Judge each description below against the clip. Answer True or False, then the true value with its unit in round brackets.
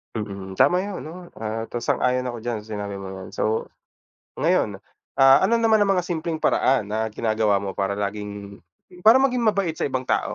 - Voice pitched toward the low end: True (115 Hz)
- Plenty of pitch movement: True (8.7 semitones)